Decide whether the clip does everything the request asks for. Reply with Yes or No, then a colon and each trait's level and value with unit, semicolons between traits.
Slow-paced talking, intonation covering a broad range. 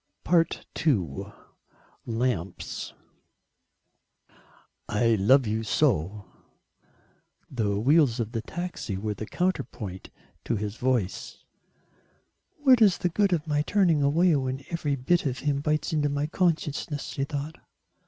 Yes: slow, 120 wpm; wide, 6.3 semitones